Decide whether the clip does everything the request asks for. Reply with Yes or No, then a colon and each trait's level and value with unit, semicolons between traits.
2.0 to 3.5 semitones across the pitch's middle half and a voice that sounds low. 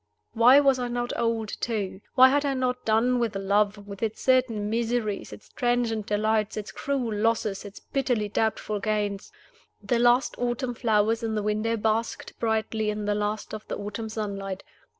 No: narrow, 2.5 semitones; high, 220 Hz